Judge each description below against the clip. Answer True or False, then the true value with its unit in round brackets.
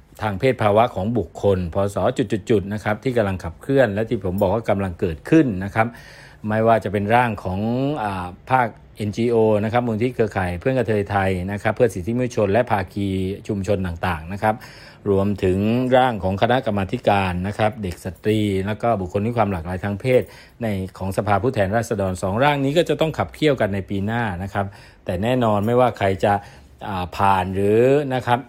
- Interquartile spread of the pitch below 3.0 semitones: False (3.4 semitones)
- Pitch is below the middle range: True (105 Hz)